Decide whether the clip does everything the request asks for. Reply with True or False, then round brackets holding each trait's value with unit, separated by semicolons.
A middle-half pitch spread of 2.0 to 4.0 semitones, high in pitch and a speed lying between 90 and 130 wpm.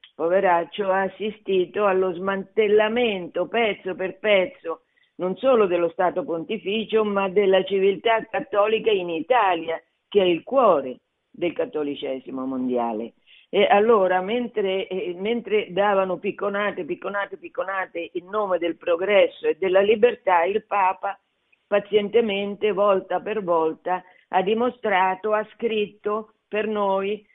True (2.7 semitones; 195 Hz; 120 wpm)